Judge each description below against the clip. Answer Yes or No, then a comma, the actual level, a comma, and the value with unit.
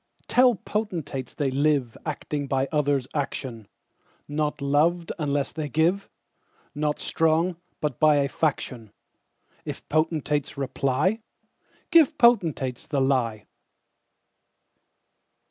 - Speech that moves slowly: Yes, slow, 80 wpm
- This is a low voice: No, medium, 150 Hz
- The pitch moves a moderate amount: Yes, average, 3.3 semitones